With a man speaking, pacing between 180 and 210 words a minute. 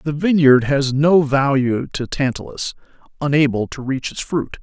No: male; average, 155 wpm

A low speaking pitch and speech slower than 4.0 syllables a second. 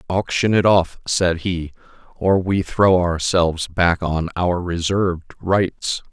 Yes: very low, 90 Hz; 3.7 syllables/s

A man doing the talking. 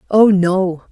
No: female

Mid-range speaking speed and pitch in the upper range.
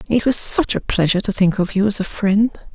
No: fast, 265 wpm; high, 205 Hz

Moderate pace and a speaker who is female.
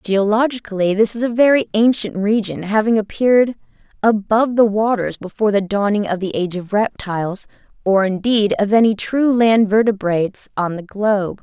Yes: average, 160 wpm; female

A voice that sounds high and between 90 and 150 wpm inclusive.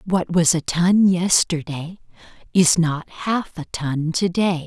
No: medium, 170 Hz; average, 140 wpm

